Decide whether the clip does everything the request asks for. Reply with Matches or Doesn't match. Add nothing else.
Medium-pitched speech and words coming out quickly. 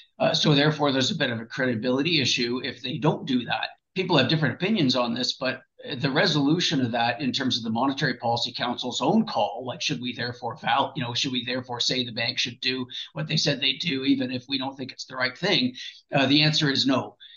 Doesn't match